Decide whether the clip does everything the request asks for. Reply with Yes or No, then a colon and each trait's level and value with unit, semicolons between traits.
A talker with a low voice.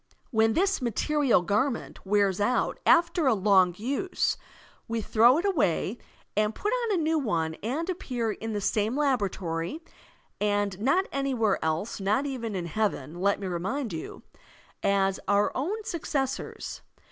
No: high, 220 Hz